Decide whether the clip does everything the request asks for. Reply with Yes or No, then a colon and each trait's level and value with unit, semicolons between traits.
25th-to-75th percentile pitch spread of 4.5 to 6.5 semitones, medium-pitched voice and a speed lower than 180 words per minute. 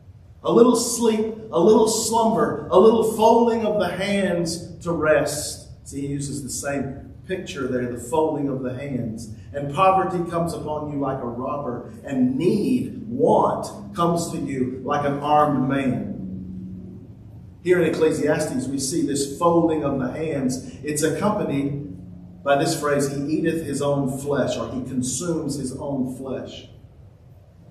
Yes: average, 4.8 semitones; medium, 145 Hz; average, 150 wpm